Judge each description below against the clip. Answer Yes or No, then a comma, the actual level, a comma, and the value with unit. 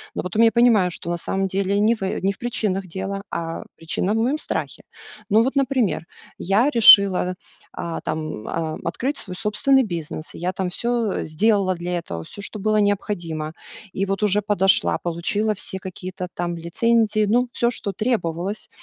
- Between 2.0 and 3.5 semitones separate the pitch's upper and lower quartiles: No, average, 3.9 semitones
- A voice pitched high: Yes, high, 195 Hz